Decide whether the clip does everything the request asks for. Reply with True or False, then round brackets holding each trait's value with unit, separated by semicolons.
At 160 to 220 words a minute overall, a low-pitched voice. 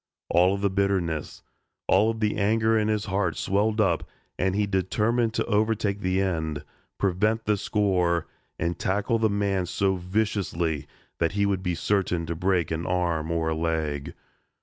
True (170 wpm; 95 Hz)